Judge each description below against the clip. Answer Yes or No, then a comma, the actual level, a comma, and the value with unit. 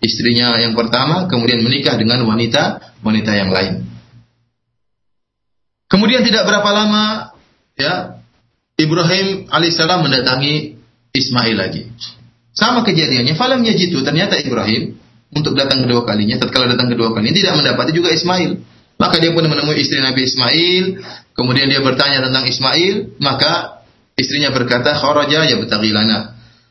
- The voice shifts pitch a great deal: Yes, wide, 5.8 semitones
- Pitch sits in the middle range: No, low, 130 Hz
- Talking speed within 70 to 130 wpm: Yes, average, 125 wpm